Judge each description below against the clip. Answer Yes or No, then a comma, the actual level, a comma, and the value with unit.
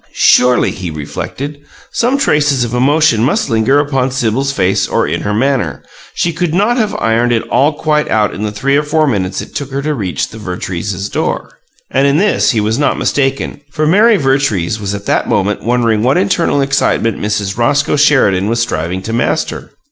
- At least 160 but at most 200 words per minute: Yes, average, 195 wpm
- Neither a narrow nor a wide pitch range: No, wide, 5.7 semitones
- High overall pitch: No, low, 125 Hz